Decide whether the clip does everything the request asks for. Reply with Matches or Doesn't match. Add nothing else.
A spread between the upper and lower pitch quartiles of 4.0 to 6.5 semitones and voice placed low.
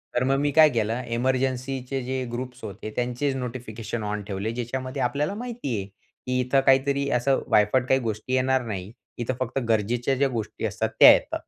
Doesn't match